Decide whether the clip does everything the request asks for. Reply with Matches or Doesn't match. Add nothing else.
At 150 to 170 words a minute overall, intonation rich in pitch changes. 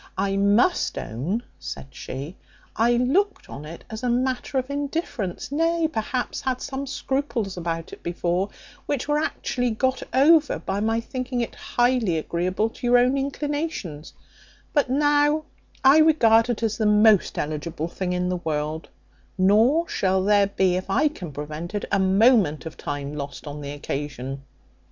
Matches